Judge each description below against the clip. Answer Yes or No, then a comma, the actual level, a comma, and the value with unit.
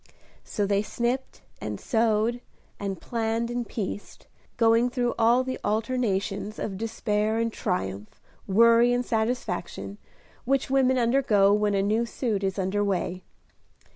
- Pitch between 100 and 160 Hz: No, high, 220 Hz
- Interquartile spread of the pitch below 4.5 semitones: Yes, average, 3.0 semitones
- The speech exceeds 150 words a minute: No, slow, 135 wpm